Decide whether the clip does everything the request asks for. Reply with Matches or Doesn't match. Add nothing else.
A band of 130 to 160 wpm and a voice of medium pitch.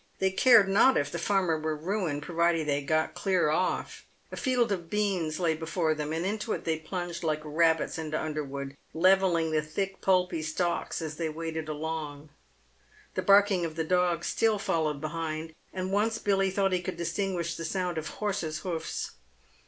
Doesn't match